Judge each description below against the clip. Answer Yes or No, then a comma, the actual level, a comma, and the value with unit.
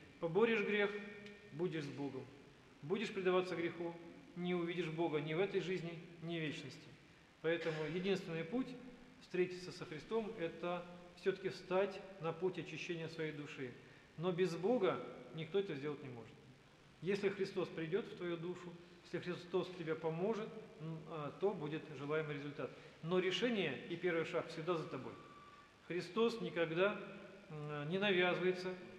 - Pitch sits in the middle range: Yes, medium, 175 Hz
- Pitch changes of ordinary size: Yes, average, 3.3 semitones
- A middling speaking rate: Yes, average, 135 wpm